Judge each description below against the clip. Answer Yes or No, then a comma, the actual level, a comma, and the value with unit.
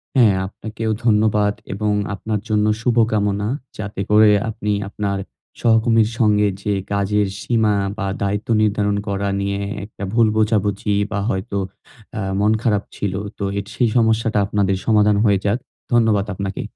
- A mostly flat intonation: Yes, narrow, 1.5 semitones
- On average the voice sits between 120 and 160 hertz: No, low, 105 Hz